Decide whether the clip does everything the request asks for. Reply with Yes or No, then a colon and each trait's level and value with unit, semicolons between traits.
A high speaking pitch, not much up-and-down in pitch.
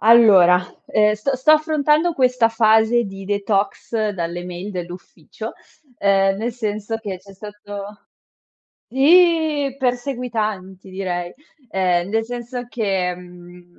No: high, 210 Hz; average, 4.5 semitones